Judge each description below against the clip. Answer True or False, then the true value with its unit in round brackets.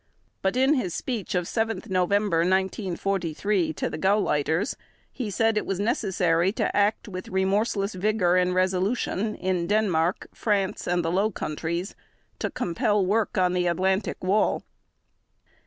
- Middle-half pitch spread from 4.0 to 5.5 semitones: False (2.9 semitones)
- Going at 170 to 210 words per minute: False (140 wpm)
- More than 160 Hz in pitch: True (190 Hz)